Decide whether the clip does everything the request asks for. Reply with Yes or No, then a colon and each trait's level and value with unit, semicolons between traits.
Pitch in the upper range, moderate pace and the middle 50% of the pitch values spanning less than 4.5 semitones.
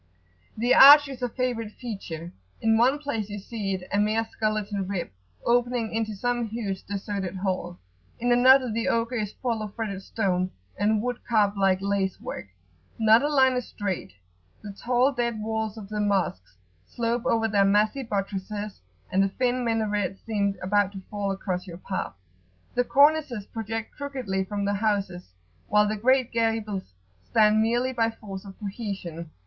Yes: high, 215 Hz; average, 165 wpm; average, 3.2 semitones